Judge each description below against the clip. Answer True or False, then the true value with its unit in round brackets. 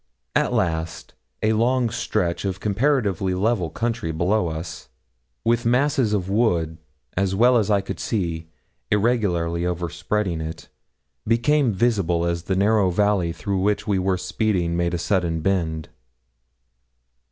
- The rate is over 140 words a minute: False (135 wpm)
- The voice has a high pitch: False (95 Hz)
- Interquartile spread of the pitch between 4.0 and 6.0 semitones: True (4.4 semitones)